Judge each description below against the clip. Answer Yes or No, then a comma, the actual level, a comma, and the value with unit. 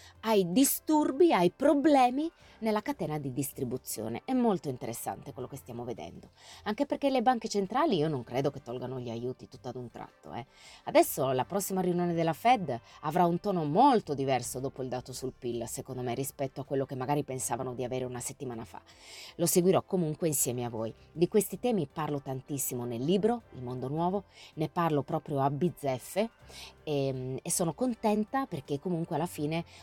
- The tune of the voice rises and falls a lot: Yes, wide, 6.9 semitones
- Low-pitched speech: No, medium, 145 Hz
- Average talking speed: No, fast, 180 wpm